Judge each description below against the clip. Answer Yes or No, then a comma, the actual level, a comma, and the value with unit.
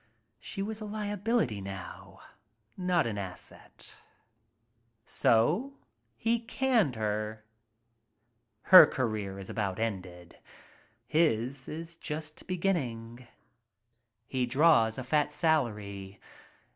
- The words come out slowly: Yes, slow, 95 wpm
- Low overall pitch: Yes, low, 130 Hz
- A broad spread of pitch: Yes, wide, 8.7 semitones